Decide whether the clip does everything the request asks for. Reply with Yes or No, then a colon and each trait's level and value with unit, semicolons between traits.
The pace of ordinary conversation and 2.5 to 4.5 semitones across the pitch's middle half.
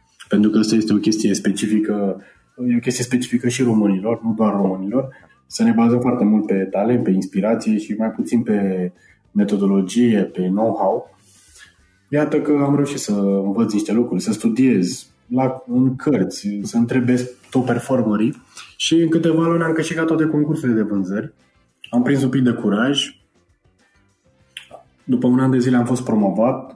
Yes: average, 160 wpm; average, 3.9 semitones